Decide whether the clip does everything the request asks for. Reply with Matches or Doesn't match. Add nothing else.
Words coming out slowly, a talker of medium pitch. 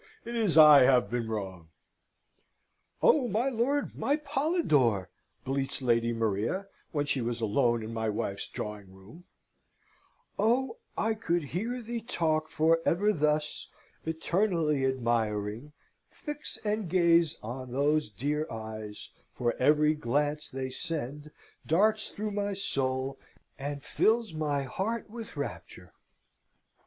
Matches